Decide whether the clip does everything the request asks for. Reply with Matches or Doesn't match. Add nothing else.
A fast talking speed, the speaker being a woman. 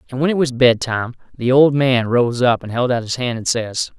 Doesn't match